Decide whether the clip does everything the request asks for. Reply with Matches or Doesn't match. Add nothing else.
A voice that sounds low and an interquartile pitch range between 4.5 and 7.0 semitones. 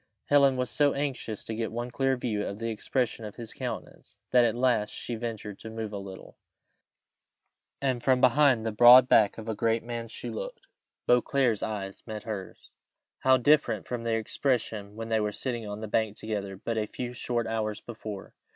Doesn't match